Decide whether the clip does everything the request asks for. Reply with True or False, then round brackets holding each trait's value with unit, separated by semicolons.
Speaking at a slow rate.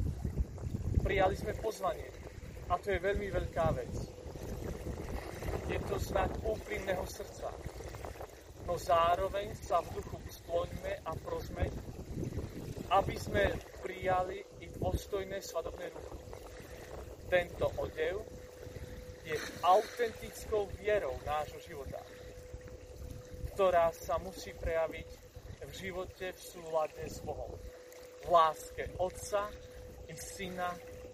True (100 wpm)